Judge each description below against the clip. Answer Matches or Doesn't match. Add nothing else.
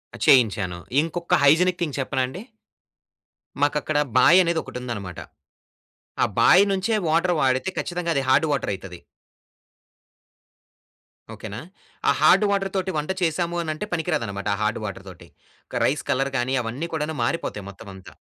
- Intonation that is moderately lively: Doesn't match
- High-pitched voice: Doesn't match